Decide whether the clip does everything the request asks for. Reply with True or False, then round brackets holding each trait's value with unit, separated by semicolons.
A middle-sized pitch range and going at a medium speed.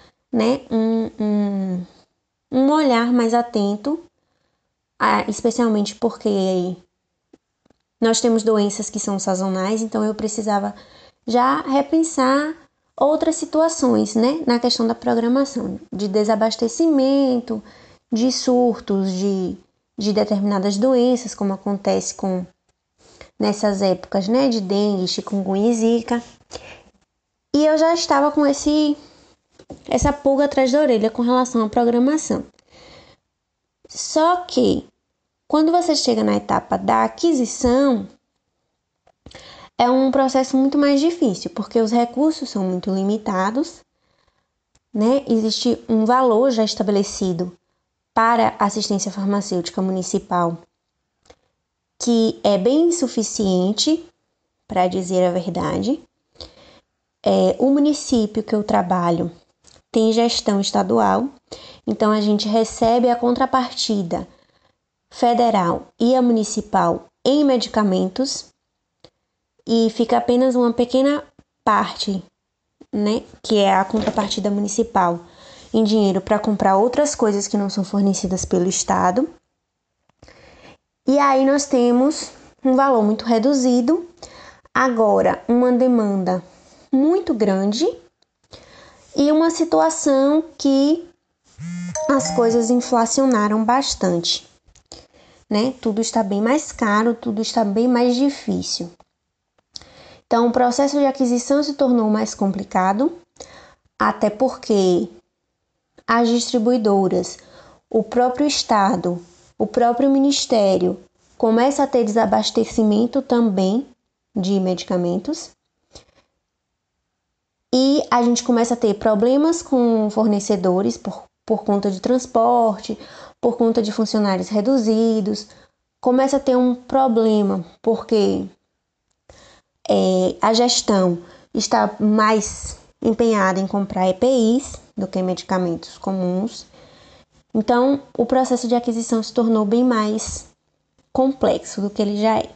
False (4.3 semitones; 105 wpm)